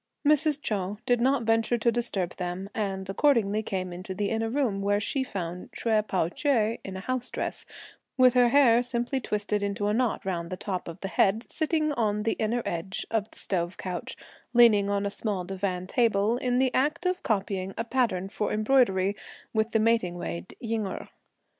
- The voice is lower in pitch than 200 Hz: No, high, 215 Hz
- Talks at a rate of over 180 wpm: Yes, average, 190 wpm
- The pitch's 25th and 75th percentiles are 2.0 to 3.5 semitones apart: No, average, 3.9 semitones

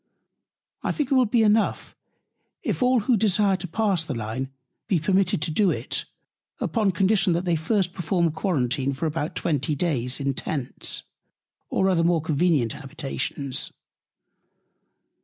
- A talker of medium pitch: Yes, medium, 170 Hz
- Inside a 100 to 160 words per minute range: Yes, average, 140 wpm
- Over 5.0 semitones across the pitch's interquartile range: Yes, wide, 5.4 semitones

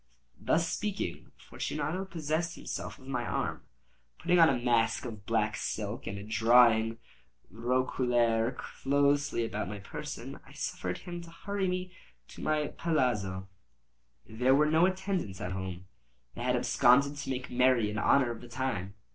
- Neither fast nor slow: Yes, average, 155 wpm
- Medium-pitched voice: No, low, 125 Hz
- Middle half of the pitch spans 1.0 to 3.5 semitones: No, wide, 5.5 semitones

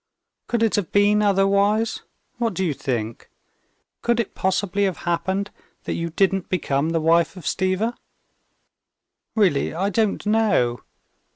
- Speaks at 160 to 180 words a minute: No, slow, 135 wpm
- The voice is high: Yes, high, 195 Hz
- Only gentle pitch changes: No, average, 3.7 semitones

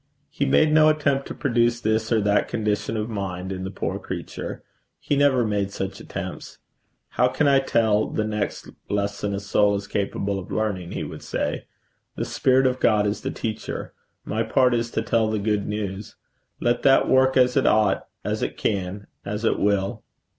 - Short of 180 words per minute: No, average, 190 wpm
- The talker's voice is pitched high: No, low, 110 Hz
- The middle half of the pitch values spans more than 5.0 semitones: No, average, 3.6 semitones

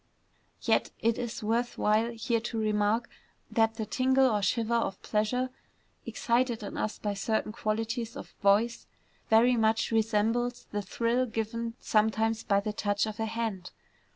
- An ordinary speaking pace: Yes, average, 155 wpm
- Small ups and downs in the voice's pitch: Yes, narrow, 1.7 semitones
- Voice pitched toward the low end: No, high, 225 Hz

